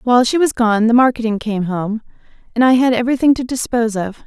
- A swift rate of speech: Yes, fast, 210 wpm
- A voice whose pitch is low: No, high, 235 Hz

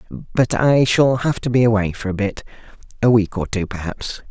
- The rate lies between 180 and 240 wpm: No, average, 165 wpm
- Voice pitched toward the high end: No, low, 110 Hz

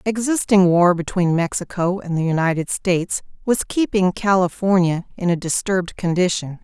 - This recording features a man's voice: No, female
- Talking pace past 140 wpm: No, slow, 135 wpm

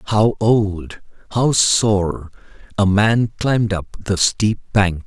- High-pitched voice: No, low, 100 Hz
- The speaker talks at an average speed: No, slow, 130 wpm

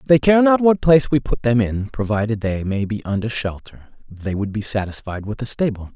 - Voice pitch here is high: No, low, 120 Hz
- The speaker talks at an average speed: No, fast, 220 wpm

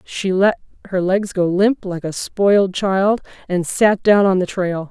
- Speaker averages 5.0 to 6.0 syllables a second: No, 4.0 syllables/s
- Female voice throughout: Yes, female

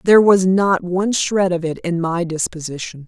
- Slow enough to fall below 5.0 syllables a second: No, 5.1 syllables/s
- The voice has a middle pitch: Yes, medium, 180 Hz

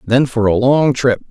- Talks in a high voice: No, low, 125 Hz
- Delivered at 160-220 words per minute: No, fast, 230 wpm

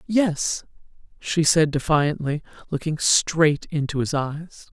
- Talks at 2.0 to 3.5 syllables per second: Yes, 3.4 syllables/s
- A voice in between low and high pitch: Yes, medium, 155 Hz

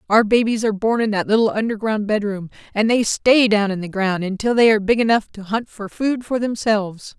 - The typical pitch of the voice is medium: No, high, 215 Hz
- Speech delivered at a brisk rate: Yes, fast, 225 wpm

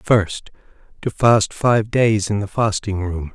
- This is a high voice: No, low, 105 Hz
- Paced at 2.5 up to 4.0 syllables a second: Yes, 3.6 syllables/s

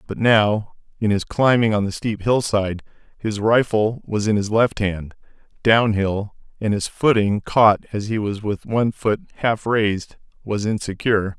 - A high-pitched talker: No, low, 105 Hz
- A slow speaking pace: No, average, 165 wpm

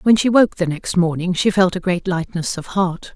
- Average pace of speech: No, fast, 245 wpm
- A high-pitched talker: No, medium, 180 Hz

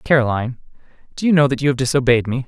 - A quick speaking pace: Yes, fast, 220 wpm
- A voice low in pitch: Yes, low, 130 Hz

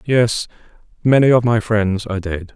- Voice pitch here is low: Yes, low, 110 Hz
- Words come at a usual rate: Yes, average, 165 wpm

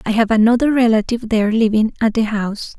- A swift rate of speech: No, average, 195 wpm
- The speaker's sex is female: Yes, female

